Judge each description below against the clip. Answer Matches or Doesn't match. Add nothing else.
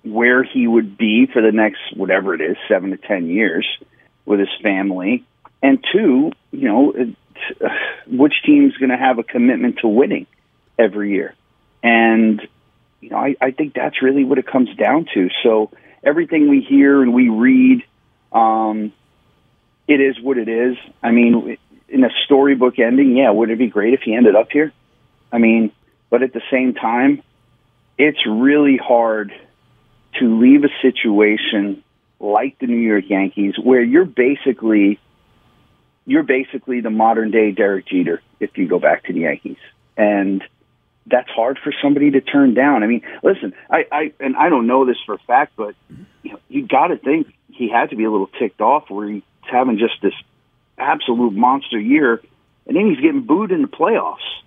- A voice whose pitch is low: Matches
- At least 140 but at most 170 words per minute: Doesn't match